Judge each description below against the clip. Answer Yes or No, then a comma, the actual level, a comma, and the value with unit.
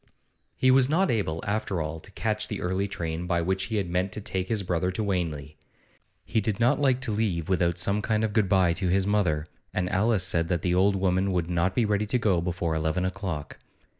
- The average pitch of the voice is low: Yes, very low, 95 Hz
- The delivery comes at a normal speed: No, fast, 225 wpm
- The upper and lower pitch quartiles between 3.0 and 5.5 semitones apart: Yes, average, 3.4 semitones